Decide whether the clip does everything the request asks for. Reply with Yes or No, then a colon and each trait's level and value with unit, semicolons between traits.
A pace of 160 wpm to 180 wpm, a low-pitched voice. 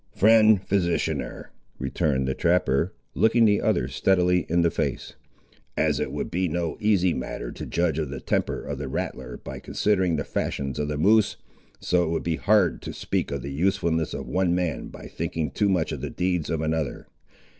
No: average, 190 wpm; very low, 85 Hz